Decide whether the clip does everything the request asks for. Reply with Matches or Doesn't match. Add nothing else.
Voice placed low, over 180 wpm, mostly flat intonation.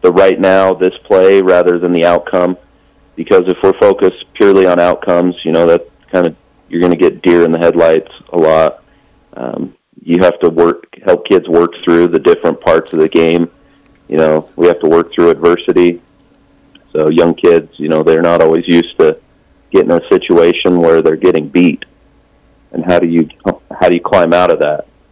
Matches